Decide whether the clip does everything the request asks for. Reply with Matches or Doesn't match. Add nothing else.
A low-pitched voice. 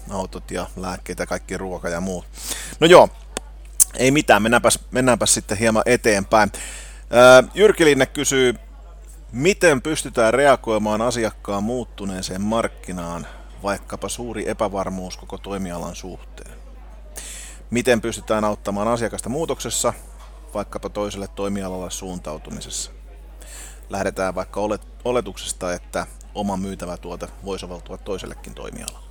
Matches